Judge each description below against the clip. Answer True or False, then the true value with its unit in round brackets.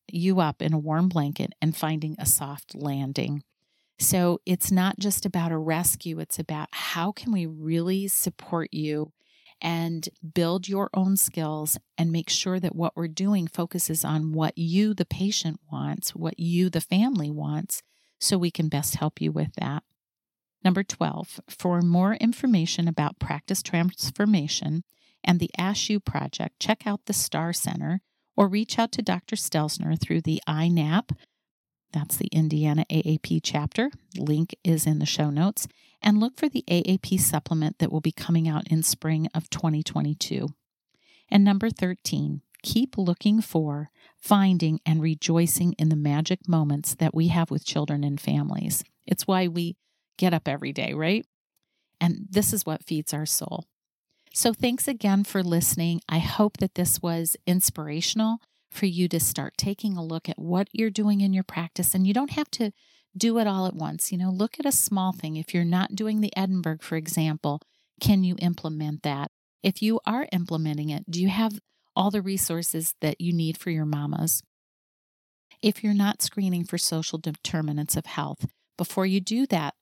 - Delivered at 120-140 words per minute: False (170 wpm)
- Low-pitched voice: False (170 Hz)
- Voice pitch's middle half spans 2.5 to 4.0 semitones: True (3.7 semitones)